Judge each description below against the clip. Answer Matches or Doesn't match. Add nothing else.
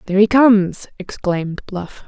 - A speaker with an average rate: Matches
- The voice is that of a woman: Matches